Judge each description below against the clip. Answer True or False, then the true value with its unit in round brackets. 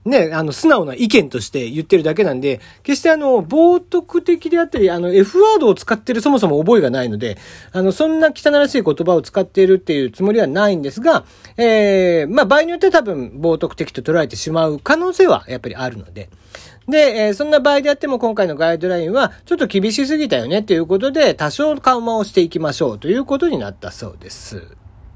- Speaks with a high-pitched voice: True (195 Hz)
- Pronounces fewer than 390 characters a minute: False (440 characters per minute)